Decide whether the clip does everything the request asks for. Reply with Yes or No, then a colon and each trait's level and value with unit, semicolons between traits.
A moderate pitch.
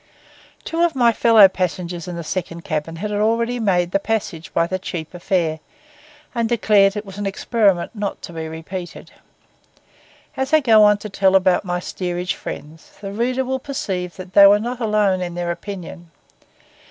No: high, 195 Hz